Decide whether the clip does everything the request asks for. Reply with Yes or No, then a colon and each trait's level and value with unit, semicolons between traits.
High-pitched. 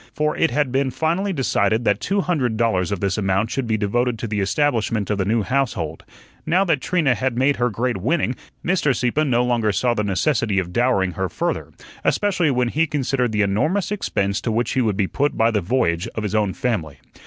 No: low, 120 Hz